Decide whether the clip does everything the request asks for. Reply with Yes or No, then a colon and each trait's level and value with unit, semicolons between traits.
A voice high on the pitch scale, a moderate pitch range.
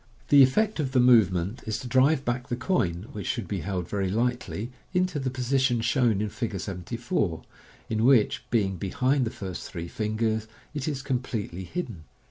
No: low, 115 Hz; average, 4.7 semitones